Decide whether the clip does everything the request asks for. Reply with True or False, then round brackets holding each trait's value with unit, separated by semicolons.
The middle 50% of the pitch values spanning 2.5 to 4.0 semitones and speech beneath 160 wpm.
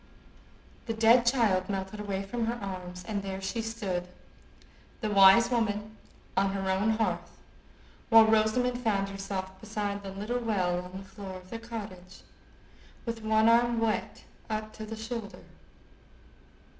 True (2.8 semitones; 145 wpm)